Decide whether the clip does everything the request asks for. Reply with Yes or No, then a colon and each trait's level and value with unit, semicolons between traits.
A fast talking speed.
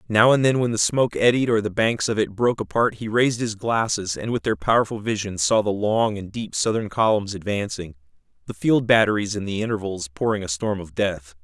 Yes: fast, 220 wpm